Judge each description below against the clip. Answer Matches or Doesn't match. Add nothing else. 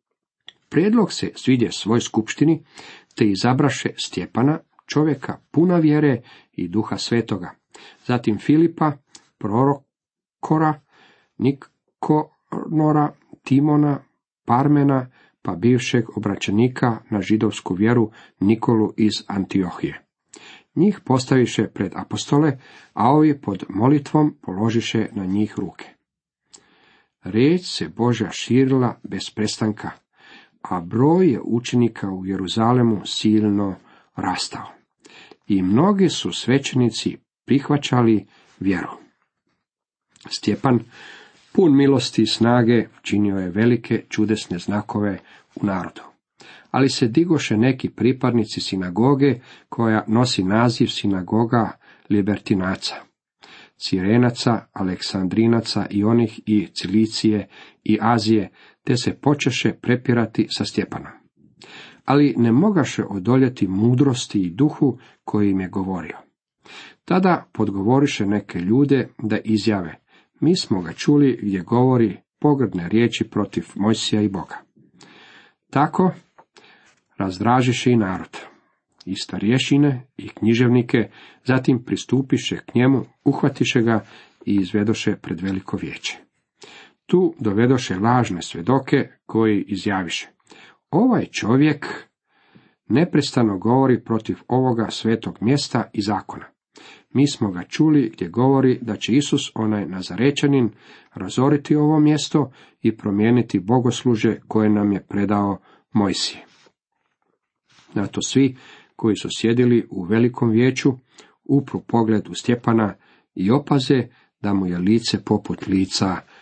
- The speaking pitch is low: Matches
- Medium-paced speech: Doesn't match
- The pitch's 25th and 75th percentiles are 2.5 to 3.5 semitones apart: Doesn't match